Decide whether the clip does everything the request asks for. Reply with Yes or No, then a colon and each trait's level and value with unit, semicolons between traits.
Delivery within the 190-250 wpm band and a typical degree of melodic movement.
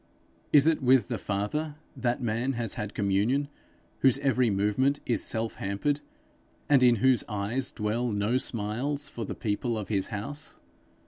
No: average, 155 wpm; average, 4.5 semitones